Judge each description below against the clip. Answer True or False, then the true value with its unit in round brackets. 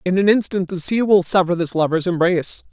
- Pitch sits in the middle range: True (180 Hz)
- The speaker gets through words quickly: True (220 wpm)